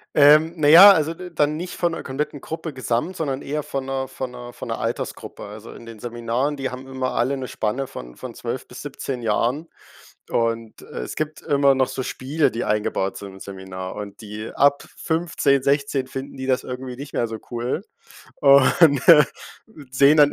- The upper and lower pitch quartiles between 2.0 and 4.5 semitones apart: Yes, average, 3.7 semitones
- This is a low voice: Yes, low, 130 Hz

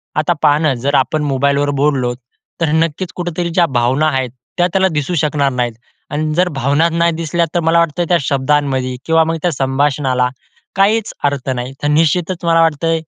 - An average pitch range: Yes, average, 3.7 semitones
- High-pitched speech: No, medium, 150 Hz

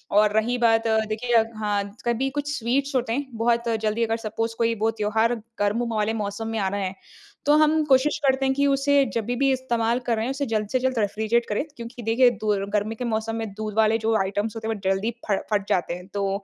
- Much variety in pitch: No, narrow, 2.6 semitones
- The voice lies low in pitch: No, high, 225 Hz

